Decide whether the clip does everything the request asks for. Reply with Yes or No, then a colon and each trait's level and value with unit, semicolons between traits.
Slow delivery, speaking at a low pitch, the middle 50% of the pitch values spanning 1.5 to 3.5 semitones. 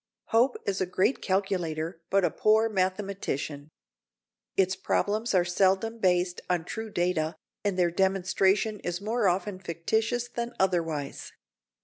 No: slow, 130 wpm; high, 190 Hz; average, 3.1 semitones